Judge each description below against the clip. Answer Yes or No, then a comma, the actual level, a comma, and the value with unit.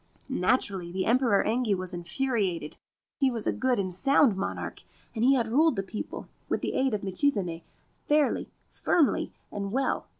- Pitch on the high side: Yes, high, 220 Hz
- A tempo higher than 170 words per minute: No, average, 160 wpm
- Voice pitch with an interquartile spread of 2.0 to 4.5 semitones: No, wide, 5.6 semitones